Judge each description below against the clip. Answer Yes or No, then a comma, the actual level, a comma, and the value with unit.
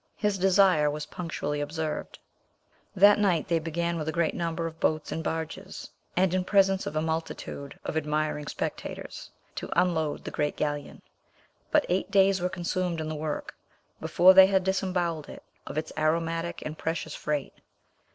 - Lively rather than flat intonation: No, average, 3.0 semitones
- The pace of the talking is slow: No, average, 165 wpm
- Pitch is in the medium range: Yes, medium, 165 Hz